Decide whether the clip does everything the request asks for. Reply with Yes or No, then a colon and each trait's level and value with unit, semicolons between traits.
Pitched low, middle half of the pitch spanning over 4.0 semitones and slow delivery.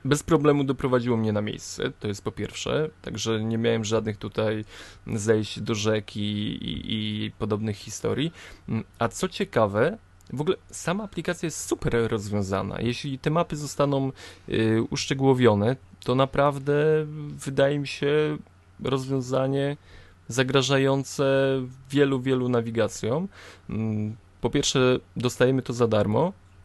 No: low, 125 Hz; average, 4.5 semitones; average, 125 wpm